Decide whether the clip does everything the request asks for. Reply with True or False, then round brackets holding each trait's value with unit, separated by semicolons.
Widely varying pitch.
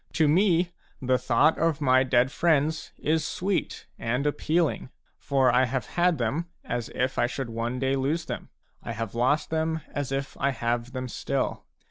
False (4.3 semitones)